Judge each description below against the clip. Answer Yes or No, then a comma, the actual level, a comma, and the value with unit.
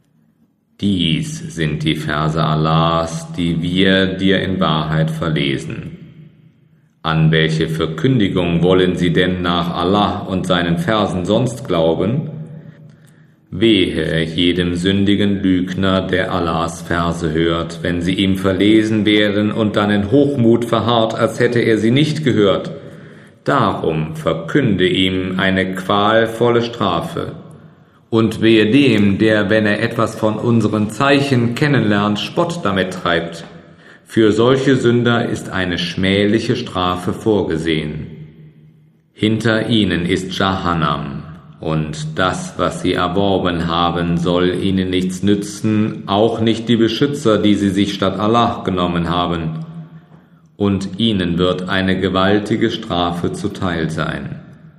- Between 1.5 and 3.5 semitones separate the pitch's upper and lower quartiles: No, average, 4.6 semitones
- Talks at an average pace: No, slow, 120 wpm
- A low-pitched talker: Yes, low, 100 Hz